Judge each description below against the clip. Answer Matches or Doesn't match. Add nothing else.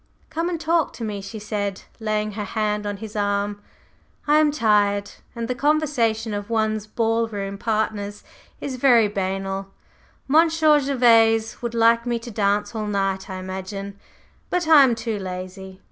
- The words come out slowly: Doesn't match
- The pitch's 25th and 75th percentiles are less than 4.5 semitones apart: Matches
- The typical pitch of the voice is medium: Doesn't match